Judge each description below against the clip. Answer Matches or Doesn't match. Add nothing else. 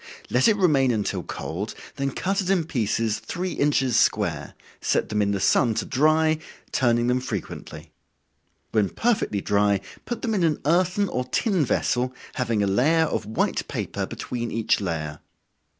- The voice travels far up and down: Matches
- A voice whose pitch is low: Matches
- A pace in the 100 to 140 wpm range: Doesn't match